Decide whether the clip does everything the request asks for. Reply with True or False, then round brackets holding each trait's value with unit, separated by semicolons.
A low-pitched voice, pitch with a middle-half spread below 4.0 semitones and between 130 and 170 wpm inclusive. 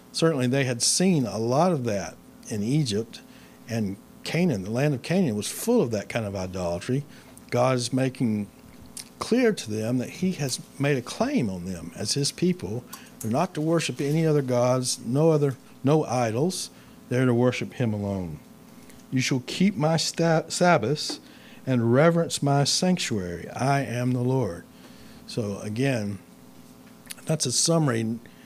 False (130 Hz; 5.5 semitones; 160 wpm)